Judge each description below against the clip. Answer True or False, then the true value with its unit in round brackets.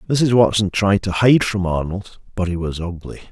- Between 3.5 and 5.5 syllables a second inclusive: True (4.8 syllables/s)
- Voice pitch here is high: False (100 Hz)